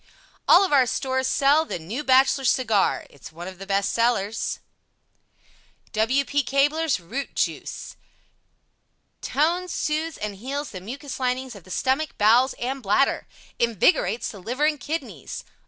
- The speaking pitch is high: Yes, very high, 260 Hz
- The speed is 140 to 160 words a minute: Yes, average, 150 wpm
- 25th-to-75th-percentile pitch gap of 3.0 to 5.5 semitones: Yes, average, 5.1 semitones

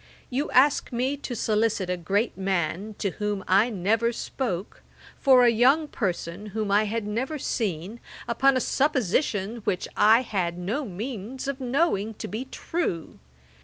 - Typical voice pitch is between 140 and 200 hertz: No, high, 220 Hz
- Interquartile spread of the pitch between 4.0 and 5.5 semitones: Yes, average, 4.7 semitones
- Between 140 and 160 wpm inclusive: Yes, average, 155 wpm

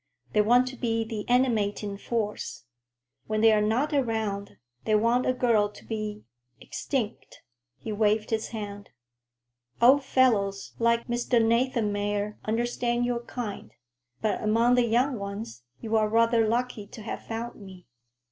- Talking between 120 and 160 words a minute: Yes, average, 140 wpm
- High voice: Yes, high, 225 Hz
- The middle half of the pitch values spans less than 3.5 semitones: Yes, narrow, 2.4 semitones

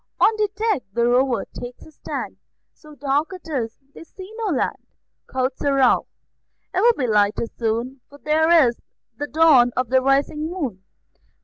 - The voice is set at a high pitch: Yes, very high, 275 Hz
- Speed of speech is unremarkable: Yes, average, 175 wpm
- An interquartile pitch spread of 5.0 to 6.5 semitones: No, average, 4.6 semitones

